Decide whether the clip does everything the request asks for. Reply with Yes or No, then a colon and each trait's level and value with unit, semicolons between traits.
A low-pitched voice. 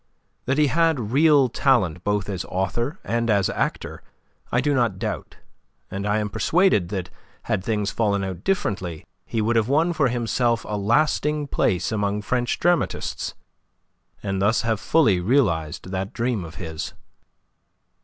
Yes: low, 110 Hz